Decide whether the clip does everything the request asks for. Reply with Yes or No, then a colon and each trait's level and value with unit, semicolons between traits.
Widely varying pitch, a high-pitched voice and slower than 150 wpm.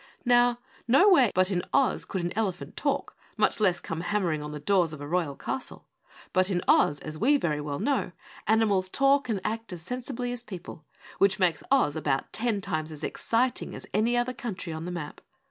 No: wide, 6.8 semitones; high, 195 Hz; average, 195 wpm